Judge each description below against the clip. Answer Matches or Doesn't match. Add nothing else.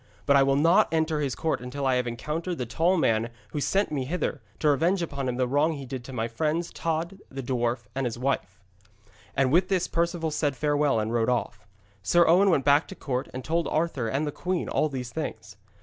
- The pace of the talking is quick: Matches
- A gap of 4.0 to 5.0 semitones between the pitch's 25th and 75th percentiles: Matches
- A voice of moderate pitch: Matches